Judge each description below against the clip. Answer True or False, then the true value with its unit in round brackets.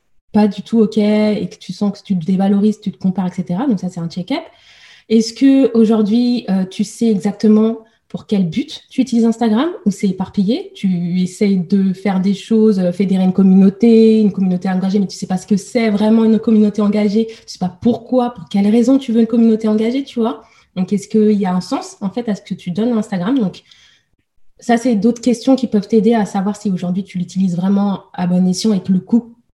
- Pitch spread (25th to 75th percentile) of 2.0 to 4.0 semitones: True (3.1 semitones)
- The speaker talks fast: True (230 wpm)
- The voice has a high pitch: True (210 Hz)